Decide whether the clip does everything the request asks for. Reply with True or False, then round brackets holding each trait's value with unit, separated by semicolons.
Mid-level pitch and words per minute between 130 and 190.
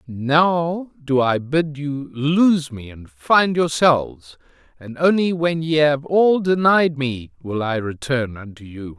True (145 Hz; 155 wpm)